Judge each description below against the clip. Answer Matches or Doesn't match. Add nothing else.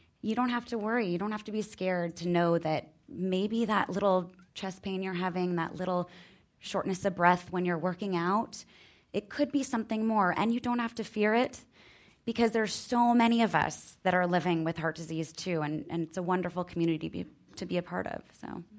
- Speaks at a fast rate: Matches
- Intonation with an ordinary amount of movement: Matches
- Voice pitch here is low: Doesn't match